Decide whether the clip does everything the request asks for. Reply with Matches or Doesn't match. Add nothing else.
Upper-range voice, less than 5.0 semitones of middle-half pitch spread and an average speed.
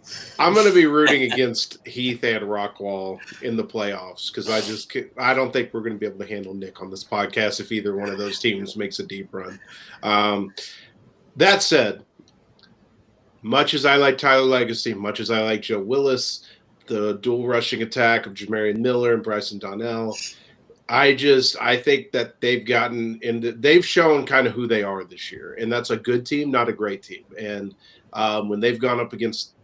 Doesn't match